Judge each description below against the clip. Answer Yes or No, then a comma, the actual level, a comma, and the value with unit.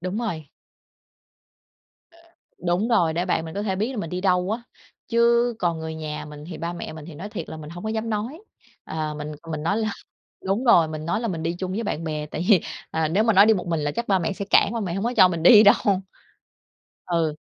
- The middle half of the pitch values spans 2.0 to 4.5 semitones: No, average, 5.0 semitones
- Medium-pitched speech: Yes, medium, 180 Hz